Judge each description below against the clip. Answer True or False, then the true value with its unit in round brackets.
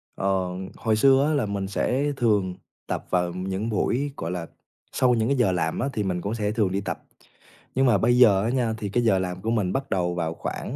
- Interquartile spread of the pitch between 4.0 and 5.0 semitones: True (4.7 semitones)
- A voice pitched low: True (105 Hz)